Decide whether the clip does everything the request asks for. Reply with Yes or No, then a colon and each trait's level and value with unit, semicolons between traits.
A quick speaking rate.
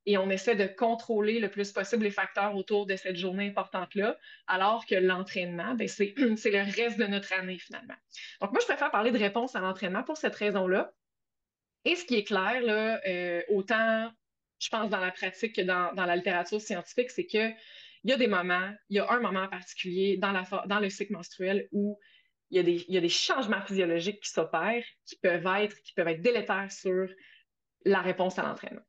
No: average, 205 wpm